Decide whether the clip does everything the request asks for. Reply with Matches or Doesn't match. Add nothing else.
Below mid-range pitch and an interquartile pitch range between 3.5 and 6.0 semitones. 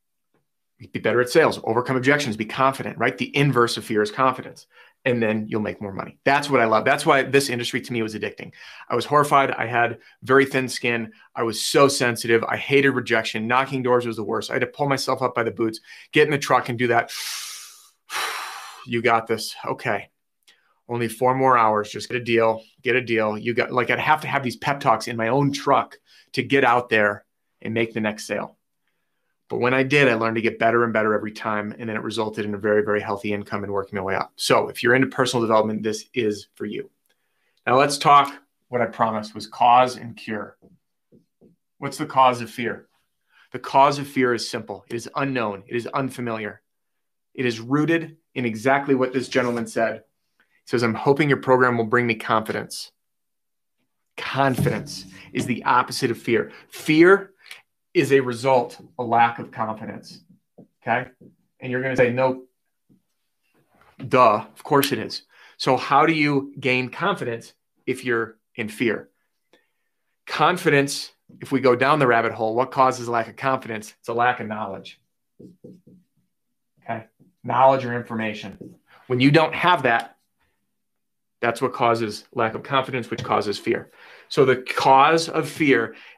Doesn't match